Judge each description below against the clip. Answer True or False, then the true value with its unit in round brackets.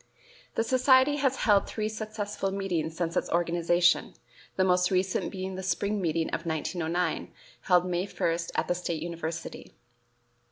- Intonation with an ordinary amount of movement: True (3.1 semitones)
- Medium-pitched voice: True (180 Hz)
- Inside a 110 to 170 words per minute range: True (150 wpm)